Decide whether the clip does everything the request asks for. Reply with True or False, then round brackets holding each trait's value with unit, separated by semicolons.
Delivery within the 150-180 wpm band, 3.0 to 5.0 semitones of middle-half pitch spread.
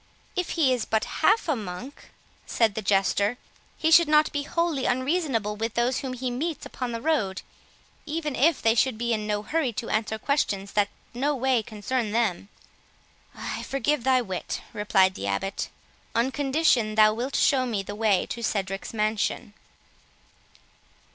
True (165 wpm; 4.6 semitones)